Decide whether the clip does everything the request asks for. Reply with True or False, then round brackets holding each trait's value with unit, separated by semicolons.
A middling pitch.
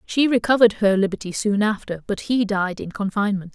False (205 Hz)